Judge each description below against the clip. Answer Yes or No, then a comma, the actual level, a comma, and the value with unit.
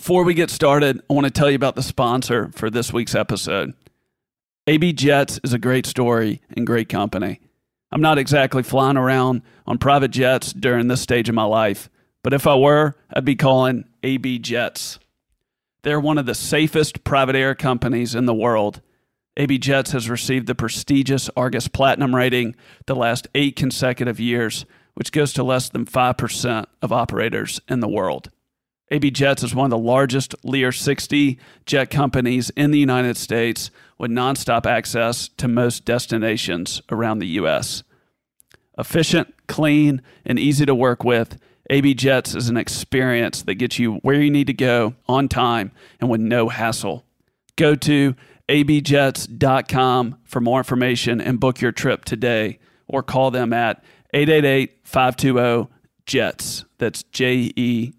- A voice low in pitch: Yes, low, 130 Hz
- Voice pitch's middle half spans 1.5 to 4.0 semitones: Yes, narrow, 2.6 semitones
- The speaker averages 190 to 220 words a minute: No, average, 155 wpm